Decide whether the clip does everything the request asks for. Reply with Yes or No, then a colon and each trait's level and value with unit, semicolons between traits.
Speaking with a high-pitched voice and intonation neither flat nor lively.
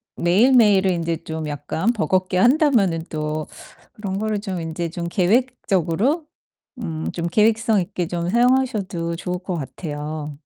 No: medium, 180 Hz; average, 4.7 semitones